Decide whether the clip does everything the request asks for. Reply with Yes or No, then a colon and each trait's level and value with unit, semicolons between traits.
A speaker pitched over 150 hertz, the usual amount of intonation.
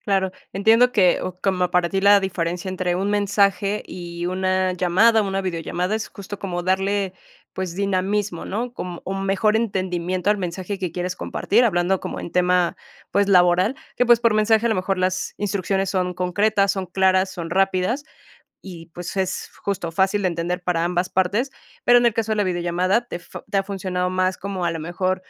No: high, 190 Hz; narrow, 2.0 semitones